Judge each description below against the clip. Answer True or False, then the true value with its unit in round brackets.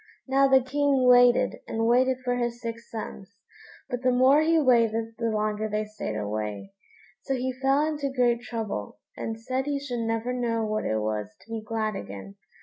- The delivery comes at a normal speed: True (185 wpm)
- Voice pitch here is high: True (235 Hz)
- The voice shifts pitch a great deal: False (3.2 semitones)